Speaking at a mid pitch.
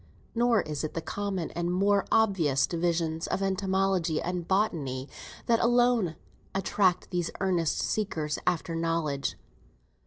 Yes: medium, 180 Hz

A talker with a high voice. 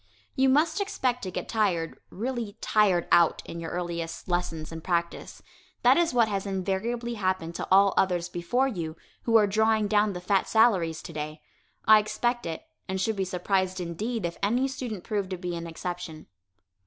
Yes: high, 195 Hz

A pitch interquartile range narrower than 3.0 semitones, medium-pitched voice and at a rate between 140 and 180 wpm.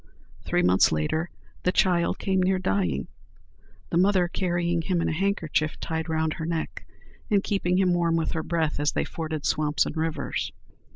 Yes: narrow, 2.5 semitones; medium, 165 Hz; average, 175 wpm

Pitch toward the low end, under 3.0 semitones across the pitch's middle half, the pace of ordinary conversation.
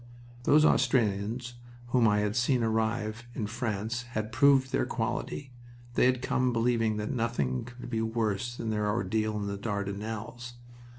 Yes: low, 115 Hz; narrow, 2.4 semitones; average, 155 wpm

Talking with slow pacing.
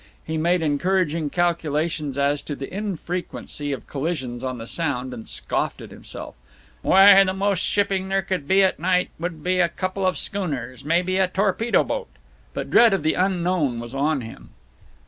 No: average, 175 wpm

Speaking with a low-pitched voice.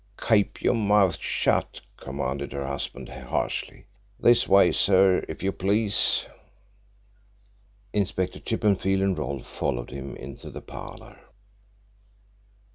Yes: very low, 95 Hz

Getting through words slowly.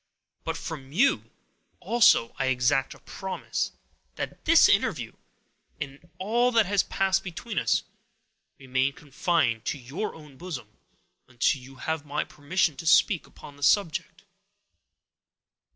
Yes: slow, 130 wpm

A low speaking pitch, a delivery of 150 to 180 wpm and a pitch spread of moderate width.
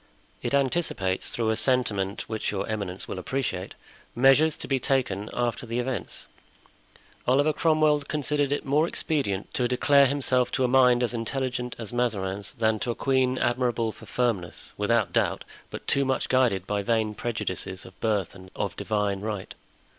Yes: low, 120 Hz; average, 165 wpm; average, 4.3 semitones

